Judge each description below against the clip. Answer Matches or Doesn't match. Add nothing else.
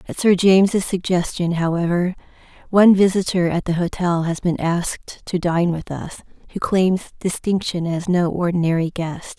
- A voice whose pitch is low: Doesn't match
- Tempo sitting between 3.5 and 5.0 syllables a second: Matches